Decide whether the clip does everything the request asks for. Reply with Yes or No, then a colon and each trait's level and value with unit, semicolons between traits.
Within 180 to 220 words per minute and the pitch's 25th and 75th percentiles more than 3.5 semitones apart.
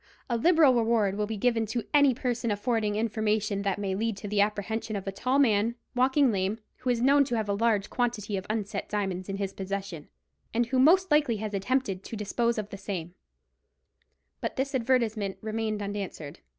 No: average, 190 wpm; average, 3.2 semitones